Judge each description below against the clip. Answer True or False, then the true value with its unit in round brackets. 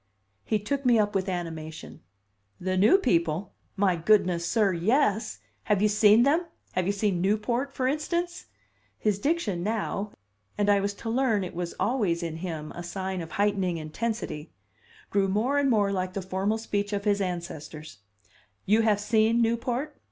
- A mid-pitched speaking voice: False (205 Hz)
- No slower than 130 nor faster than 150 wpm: False (165 wpm)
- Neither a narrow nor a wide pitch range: True (3.9 semitones)